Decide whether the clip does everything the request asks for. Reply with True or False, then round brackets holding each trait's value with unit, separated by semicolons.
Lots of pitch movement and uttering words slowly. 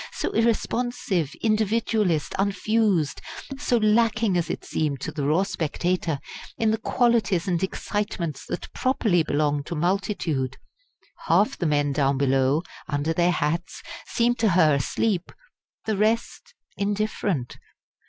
True (6.1 semitones; 125 wpm)